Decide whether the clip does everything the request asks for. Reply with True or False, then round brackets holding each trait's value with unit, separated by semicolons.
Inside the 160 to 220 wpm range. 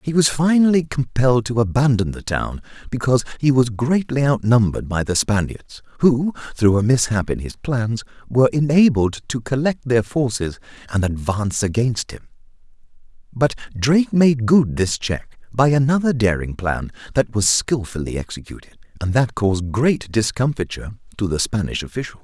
False (150 wpm)